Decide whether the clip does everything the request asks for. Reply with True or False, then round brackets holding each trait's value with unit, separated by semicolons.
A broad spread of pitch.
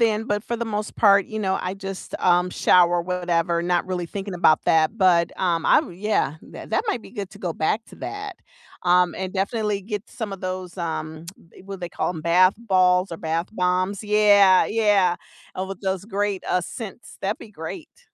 False (2.8 semitones)